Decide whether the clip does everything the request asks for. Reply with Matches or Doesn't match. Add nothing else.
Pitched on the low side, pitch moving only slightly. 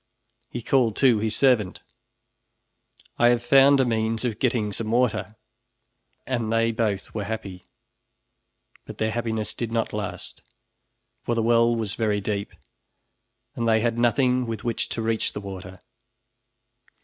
Matches